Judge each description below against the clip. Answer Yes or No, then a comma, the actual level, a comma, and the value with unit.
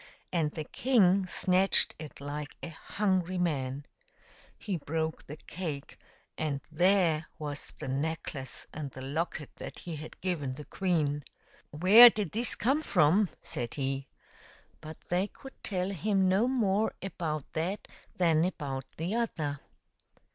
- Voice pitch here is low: No, medium, 165 Hz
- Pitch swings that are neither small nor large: Yes, average, 4.5 semitones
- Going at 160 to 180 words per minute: No, average, 145 wpm